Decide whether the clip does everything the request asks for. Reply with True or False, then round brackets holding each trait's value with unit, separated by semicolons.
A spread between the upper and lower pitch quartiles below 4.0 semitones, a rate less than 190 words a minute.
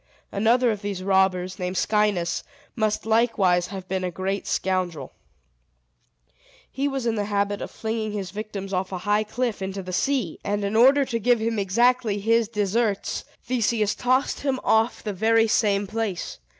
True (3.1 semitones; 170 wpm)